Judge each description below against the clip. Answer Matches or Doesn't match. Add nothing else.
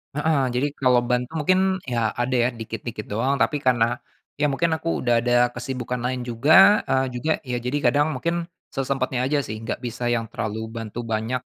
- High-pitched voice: Doesn't match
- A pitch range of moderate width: Matches